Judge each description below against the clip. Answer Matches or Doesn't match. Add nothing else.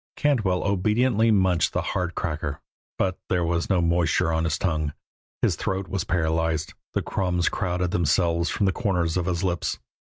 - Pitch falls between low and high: Doesn't match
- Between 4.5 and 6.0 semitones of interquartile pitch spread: Doesn't match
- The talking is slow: Doesn't match